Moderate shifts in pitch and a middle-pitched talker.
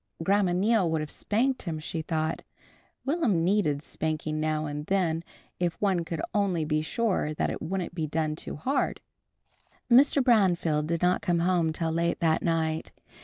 Yes: average, 3.5 semitones; medium, 170 Hz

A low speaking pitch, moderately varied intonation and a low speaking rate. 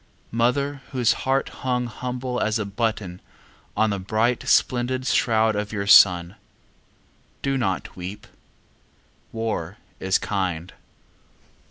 Yes: low, 110 Hz; average, 3.9 semitones; slow, 115 wpm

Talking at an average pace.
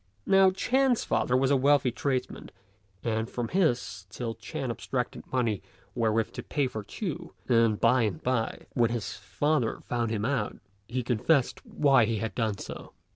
Yes: average, 165 wpm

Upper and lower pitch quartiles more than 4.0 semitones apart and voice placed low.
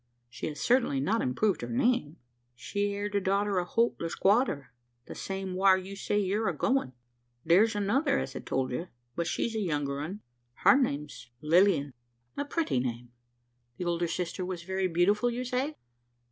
No: average, 5.2 semitones; high, 190 Hz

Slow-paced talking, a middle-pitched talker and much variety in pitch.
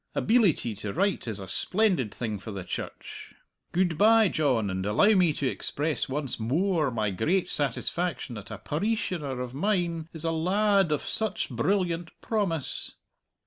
No: average, 160 wpm; medium, 160 Hz; wide, 7.9 semitones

